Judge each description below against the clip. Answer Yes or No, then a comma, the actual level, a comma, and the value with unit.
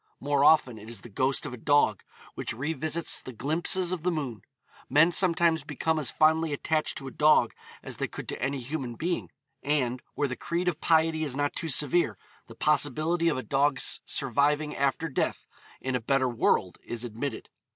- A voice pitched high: No, medium, 145 Hz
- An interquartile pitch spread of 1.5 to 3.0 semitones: No, average, 3.7 semitones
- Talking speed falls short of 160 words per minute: No, average, 190 wpm